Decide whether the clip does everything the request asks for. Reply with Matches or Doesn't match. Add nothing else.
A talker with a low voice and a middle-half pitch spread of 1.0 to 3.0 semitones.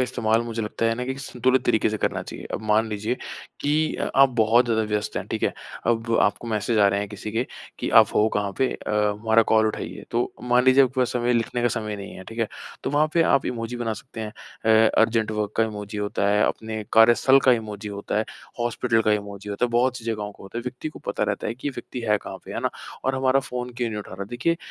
Matches